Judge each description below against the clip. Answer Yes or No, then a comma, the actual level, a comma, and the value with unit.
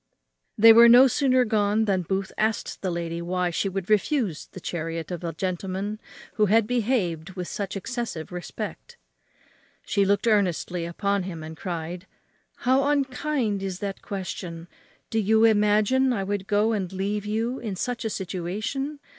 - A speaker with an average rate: Yes, average, 160 wpm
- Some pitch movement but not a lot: Yes, average, 3.9 semitones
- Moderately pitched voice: No, high, 200 Hz